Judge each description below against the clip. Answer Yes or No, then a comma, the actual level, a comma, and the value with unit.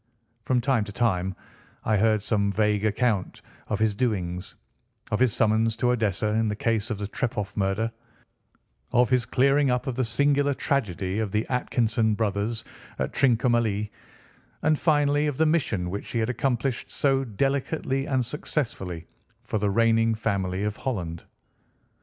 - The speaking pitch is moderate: No, low, 115 Hz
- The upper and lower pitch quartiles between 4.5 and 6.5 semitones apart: No, average, 3.8 semitones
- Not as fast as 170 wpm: Yes, average, 155 wpm